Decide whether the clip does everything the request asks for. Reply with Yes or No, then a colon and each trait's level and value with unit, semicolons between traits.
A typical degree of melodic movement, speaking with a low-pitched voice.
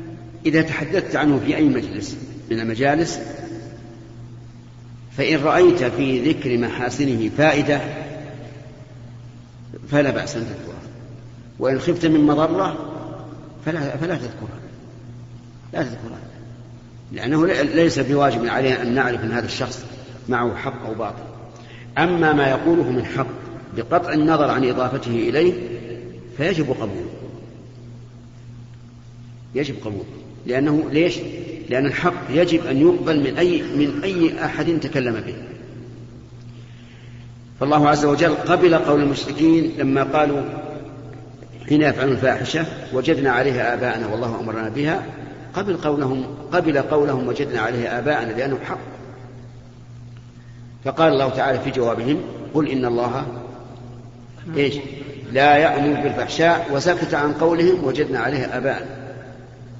Yes: average, 3.7 semitones; low, 130 Hz